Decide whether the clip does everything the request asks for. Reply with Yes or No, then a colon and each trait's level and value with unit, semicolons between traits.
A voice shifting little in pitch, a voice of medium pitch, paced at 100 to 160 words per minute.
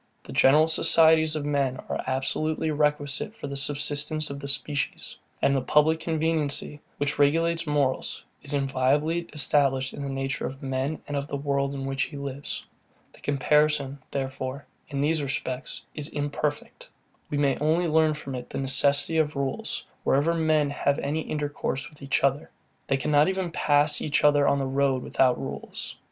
No: narrow, 1.9 semitones; medium, 145 Hz; average, 170 wpm